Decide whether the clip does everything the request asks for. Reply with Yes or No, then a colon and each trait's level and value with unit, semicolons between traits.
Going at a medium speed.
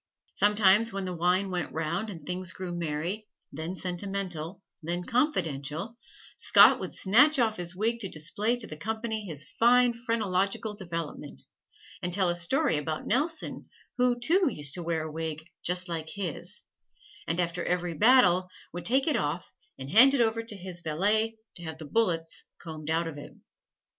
Yes: average, 170 wpm